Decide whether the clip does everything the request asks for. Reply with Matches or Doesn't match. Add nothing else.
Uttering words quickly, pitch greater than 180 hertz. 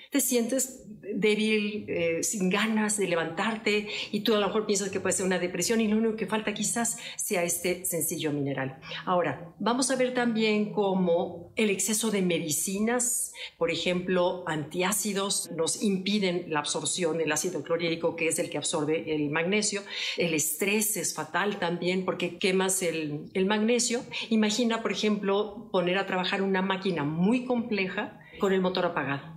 Doesn't match